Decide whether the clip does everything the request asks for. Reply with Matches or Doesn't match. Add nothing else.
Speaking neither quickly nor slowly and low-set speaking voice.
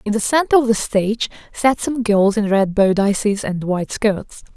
Doesn't match